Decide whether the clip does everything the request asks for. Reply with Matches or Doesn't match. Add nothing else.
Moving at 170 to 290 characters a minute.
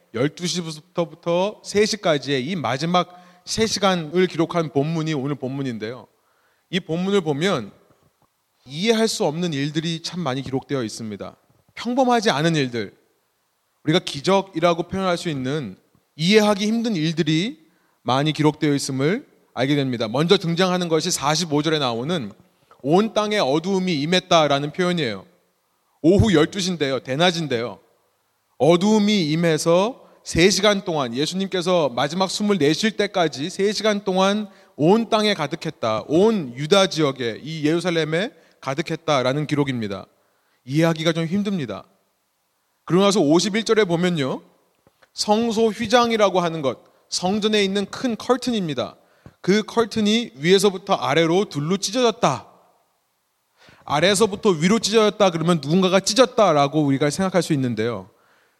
Doesn't match